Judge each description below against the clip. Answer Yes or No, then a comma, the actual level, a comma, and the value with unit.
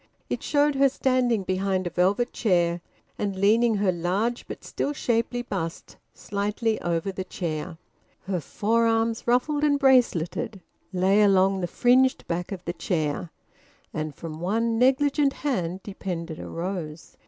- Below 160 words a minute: Yes, average, 140 wpm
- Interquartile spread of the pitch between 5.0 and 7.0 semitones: Yes, wide, 5.4 semitones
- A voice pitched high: Yes, high, 200 Hz